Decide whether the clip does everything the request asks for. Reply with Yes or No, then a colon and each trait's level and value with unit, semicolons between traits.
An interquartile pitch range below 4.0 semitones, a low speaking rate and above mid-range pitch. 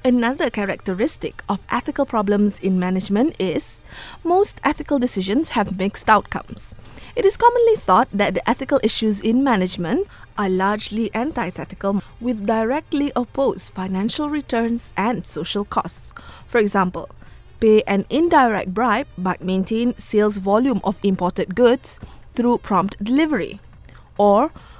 No: average, 4.8 semitones; slow, 125 wpm; high, 220 Hz